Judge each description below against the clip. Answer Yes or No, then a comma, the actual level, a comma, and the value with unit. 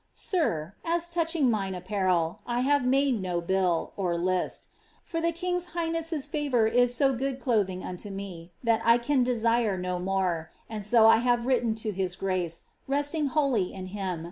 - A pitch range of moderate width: No, wide, 6.9 semitones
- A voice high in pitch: Yes, high, 225 Hz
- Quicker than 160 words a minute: Yes, average, 170 wpm